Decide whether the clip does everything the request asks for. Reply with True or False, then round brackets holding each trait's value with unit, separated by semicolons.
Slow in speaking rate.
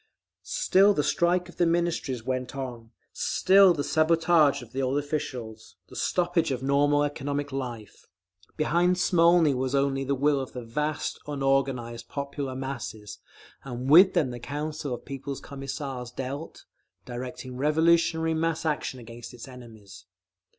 False (145 wpm)